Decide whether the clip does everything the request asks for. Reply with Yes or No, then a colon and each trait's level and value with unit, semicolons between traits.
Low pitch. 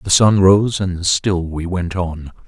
Yes: very low, 90 Hz